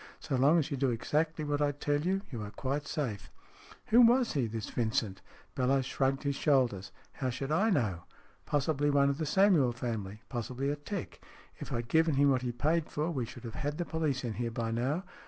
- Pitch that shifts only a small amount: No, average, 4.0 semitones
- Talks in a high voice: No, medium, 140 Hz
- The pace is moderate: No, fast, 230 wpm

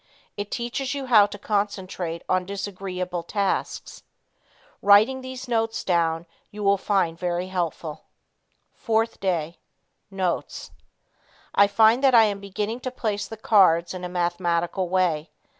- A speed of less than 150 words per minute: Yes, slow, 135 wpm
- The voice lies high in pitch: Yes, high, 195 Hz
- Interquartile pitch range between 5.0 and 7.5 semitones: No, average, 3.7 semitones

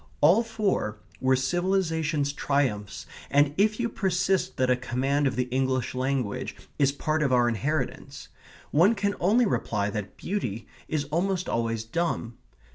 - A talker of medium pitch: Yes, medium, 145 Hz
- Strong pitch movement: Yes, wide, 6.3 semitones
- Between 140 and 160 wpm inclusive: Yes, average, 145 wpm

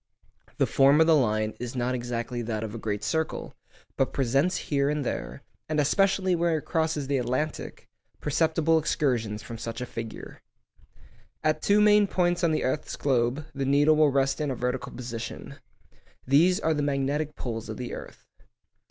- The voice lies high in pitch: No, medium, 140 Hz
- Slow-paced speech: No, average, 170 wpm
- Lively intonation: No, average, 4.4 semitones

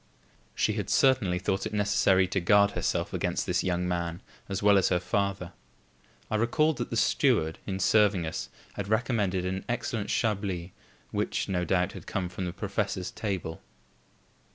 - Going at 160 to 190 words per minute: Yes, average, 165 wpm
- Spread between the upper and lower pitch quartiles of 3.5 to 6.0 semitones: No, narrow, 2.6 semitones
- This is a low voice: Yes, very low, 95 Hz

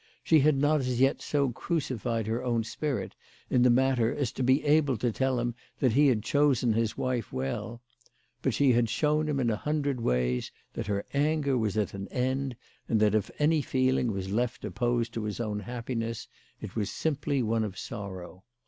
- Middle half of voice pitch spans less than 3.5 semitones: No, average, 3.9 semitones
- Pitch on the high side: No, low, 120 Hz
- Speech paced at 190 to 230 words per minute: Yes, average, 195 wpm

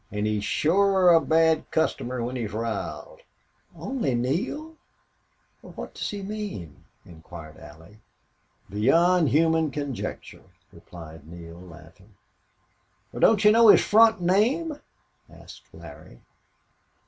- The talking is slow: Yes, slow, 110 wpm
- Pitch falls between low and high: Yes, medium, 150 Hz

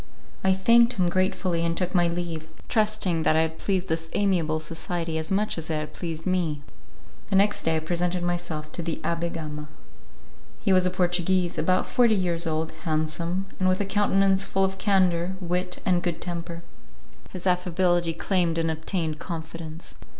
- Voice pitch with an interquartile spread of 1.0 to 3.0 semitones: Yes, narrow, 2.4 semitones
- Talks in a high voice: No, medium, 175 Hz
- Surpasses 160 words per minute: Yes, average, 175 wpm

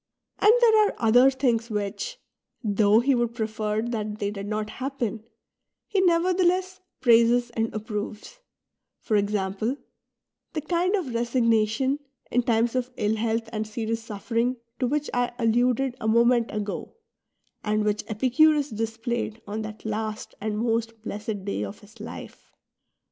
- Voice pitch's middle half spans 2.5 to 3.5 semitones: Yes, average, 3.0 semitones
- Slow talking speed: No, average, 145 wpm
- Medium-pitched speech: No, high, 230 Hz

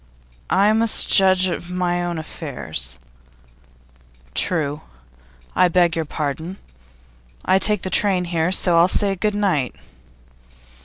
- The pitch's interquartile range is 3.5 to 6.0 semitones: No, average, 3.0 semitones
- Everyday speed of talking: No, slow, 120 wpm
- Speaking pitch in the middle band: Yes, medium, 175 Hz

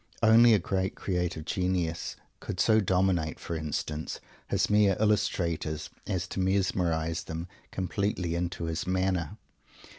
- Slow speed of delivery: Yes, slow, 125 wpm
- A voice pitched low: Yes, very low, 90 Hz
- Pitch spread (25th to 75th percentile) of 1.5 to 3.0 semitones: Yes, narrow, 2.6 semitones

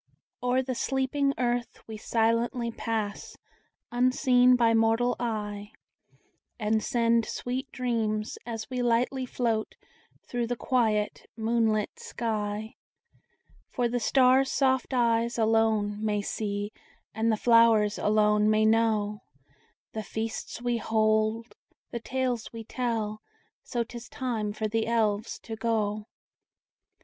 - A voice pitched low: No, high, 225 Hz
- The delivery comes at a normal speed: No, slow, 120 wpm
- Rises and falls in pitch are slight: Yes, narrow, 2.1 semitones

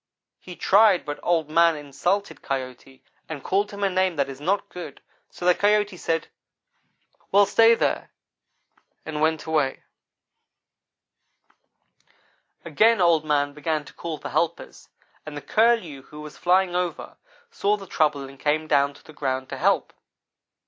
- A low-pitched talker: No, medium, 160 Hz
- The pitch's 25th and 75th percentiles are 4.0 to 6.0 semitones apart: Yes, average, 4.3 semitones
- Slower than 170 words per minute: Yes, average, 150 wpm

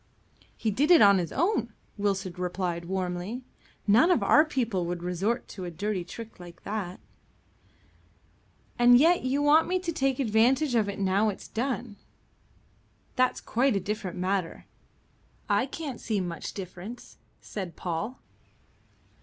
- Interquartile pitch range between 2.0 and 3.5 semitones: No, wide, 5.6 semitones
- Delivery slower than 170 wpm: Yes, average, 145 wpm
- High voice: Yes, high, 210 Hz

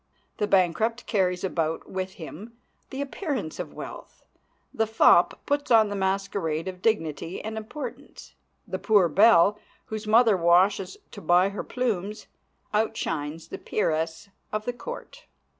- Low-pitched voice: No, high, 200 Hz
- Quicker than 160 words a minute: No, average, 140 wpm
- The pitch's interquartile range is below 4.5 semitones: Yes, average, 3.9 semitones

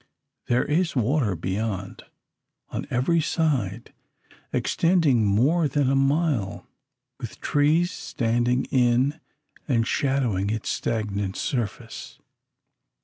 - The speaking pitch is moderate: No, low, 125 Hz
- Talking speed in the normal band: No, slow, 95 wpm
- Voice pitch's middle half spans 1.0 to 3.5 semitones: No, average, 5.1 semitones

